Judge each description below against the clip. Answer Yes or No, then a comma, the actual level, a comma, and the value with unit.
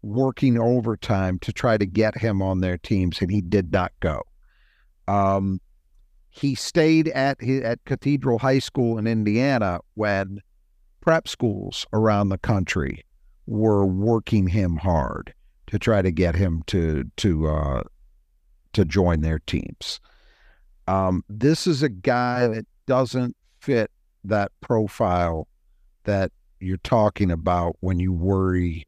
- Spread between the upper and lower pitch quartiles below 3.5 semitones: No, average, 4.7 semitones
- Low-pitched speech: Yes, low, 100 Hz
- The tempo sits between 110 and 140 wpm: Yes, slow, 135 wpm